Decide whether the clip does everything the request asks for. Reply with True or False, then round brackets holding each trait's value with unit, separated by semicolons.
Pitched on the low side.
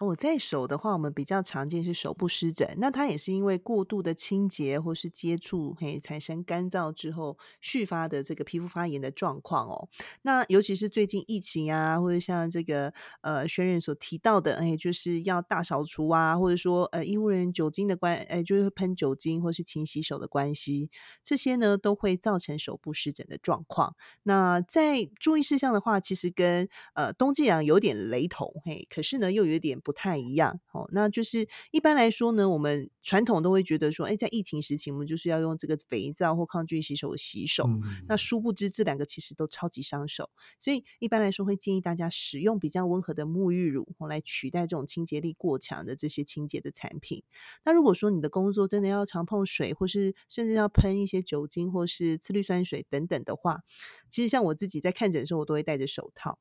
False (175 Hz)